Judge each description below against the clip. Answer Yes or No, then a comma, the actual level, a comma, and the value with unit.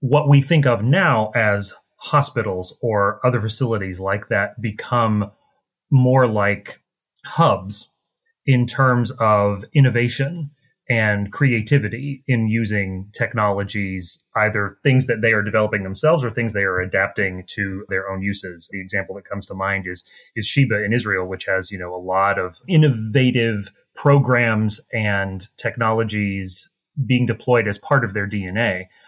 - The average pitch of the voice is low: Yes, low, 110 Hz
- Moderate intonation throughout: Yes, average, 4.1 semitones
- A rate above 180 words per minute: No, average, 145 wpm